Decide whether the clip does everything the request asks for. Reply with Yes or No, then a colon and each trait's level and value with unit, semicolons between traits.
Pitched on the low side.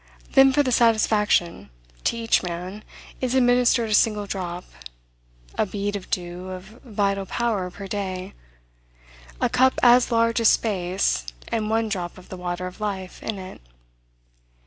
No: high, 205 Hz